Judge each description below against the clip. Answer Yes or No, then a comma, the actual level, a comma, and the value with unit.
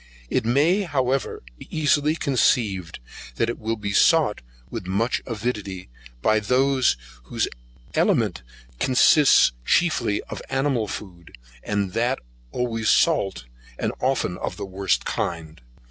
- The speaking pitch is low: Yes, low, 115 Hz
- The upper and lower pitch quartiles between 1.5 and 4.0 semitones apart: No, wide, 5.4 semitones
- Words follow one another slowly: Yes, slow, 125 wpm